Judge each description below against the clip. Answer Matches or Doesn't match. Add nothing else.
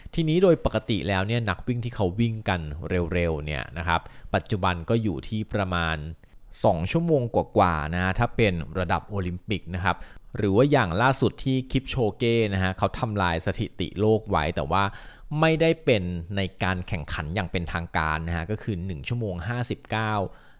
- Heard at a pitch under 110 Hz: Matches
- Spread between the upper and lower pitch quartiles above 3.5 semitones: Matches